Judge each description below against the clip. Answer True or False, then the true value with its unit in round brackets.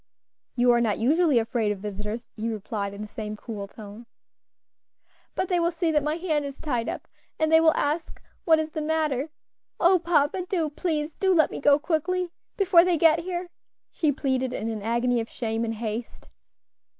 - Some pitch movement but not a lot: False (6.3 semitones)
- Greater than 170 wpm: True (190 wpm)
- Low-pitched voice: False (290 Hz)